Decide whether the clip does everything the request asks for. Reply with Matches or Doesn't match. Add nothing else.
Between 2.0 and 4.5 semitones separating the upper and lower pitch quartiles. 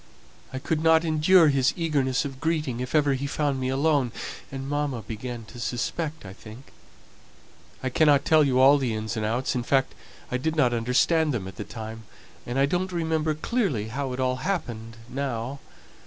Matches